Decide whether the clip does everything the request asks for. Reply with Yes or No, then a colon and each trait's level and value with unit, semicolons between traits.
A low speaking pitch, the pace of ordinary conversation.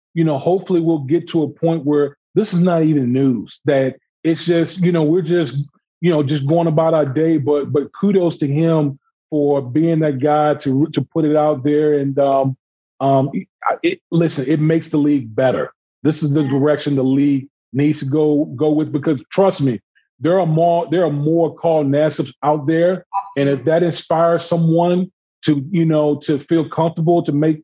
No: medium, 155 Hz; average, 195 wpm